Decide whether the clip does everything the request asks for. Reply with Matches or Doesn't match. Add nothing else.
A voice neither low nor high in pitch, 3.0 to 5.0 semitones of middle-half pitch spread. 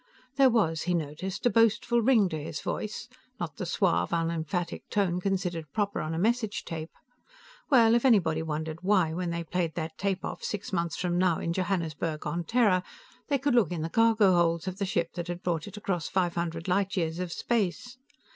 Matches